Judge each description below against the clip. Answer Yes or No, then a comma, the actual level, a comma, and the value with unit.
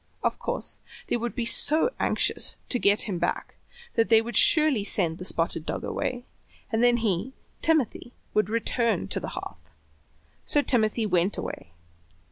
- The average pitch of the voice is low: No, high, 230 Hz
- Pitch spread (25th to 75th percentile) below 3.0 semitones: No, average, 3.4 semitones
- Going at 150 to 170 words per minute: Yes, average, 155 wpm